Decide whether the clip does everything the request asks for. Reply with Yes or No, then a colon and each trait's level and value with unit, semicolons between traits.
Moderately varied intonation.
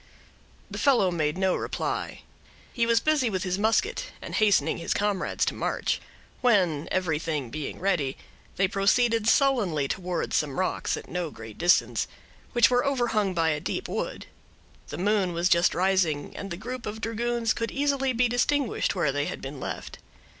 No: wide, 5.8 semitones